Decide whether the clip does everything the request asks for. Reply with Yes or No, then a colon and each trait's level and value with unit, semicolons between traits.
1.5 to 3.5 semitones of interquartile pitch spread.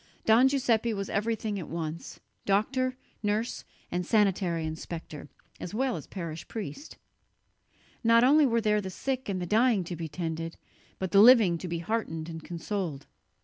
No: wide, 5.4 semitones